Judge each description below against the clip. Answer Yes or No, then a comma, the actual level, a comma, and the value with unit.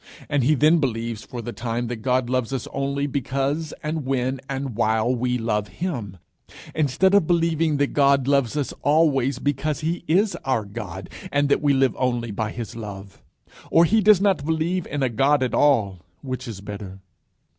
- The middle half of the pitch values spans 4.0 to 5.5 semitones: Yes, average, 4.3 semitones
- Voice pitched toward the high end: No, low, 135 Hz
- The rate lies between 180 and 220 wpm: Yes, average, 185 wpm